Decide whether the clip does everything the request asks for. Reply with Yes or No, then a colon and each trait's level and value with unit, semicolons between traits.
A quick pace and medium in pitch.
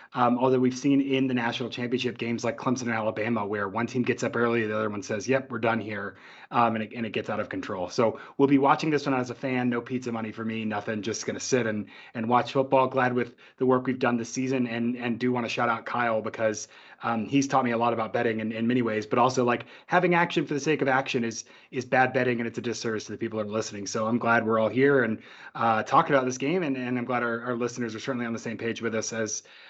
No: fast, 280 wpm; low, 120 Hz